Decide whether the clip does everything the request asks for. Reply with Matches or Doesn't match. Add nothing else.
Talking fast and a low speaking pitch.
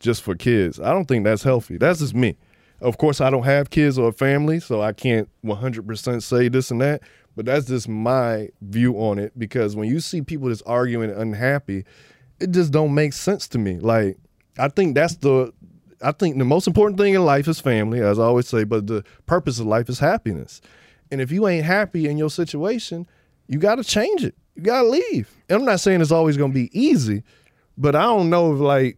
Matches